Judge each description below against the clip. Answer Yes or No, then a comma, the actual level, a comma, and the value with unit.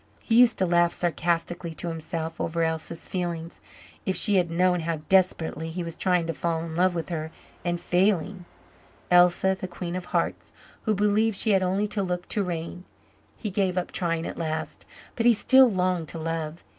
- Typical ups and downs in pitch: No, narrow, 2.3 semitones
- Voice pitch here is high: No, medium, 175 Hz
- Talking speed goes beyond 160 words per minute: Yes, average, 190 wpm